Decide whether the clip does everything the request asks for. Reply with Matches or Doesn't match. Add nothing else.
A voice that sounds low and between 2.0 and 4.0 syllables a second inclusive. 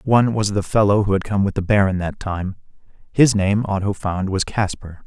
Doesn't match